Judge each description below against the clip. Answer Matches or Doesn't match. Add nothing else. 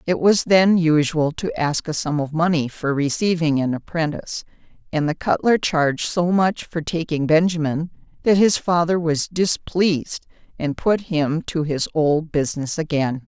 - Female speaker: Matches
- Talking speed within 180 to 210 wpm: Doesn't match